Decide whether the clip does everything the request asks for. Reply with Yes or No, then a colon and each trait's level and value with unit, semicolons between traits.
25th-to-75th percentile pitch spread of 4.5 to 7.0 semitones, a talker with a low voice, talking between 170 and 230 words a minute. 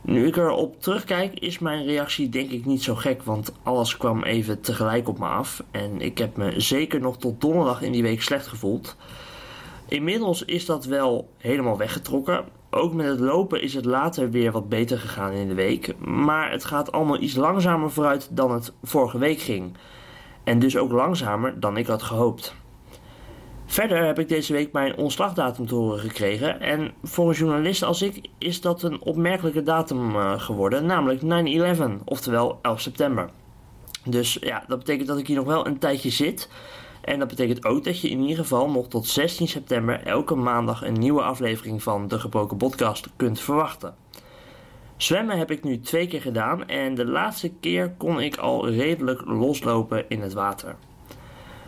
Yes: average, 5.1 semitones; low, 130 Hz; average, 180 wpm